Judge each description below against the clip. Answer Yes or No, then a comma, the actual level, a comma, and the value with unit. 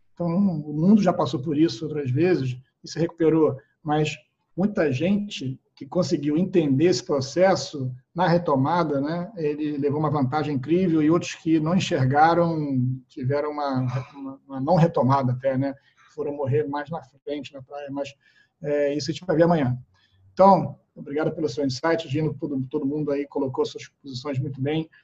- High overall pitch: No, medium, 150 Hz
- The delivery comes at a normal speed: Yes, average, 175 wpm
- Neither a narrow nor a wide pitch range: Yes, average, 3.3 semitones